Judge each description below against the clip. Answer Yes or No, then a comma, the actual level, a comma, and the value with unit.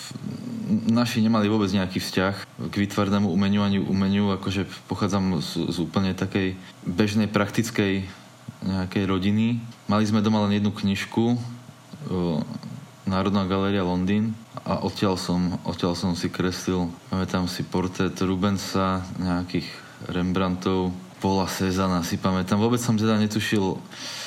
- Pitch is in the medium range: No, very low, 95 Hz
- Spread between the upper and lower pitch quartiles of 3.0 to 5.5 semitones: No, narrow, 2.4 semitones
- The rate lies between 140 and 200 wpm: No, average, 125 wpm